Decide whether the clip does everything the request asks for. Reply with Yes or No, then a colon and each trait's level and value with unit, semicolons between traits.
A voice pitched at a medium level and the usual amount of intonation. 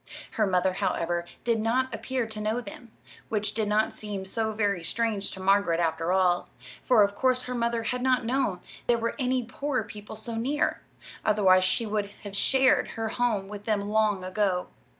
No: high, 215 Hz; average, 3.2 semitones